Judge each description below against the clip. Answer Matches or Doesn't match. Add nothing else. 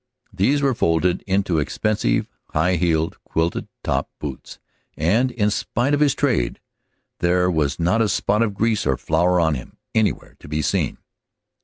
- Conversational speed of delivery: Matches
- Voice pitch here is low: Matches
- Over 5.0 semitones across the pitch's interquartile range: Matches